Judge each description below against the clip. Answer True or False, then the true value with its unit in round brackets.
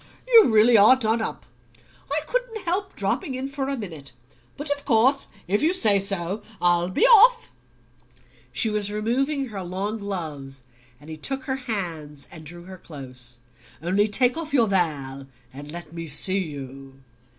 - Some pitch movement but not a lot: False (8.7 semitones)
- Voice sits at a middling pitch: False (200 Hz)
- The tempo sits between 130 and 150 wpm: False (165 wpm)